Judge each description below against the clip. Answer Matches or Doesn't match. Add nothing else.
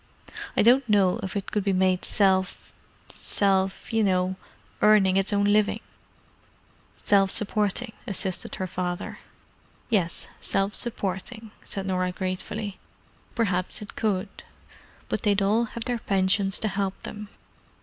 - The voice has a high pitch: Matches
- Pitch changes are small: Matches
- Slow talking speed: Matches